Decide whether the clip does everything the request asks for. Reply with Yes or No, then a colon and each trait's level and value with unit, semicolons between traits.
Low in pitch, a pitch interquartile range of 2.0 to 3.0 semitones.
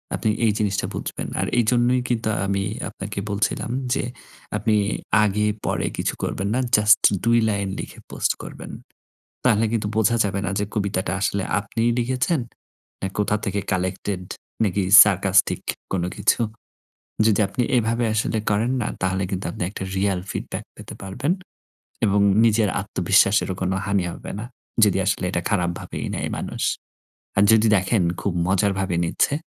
Yes: low, 105 Hz; narrow, 2.4 semitones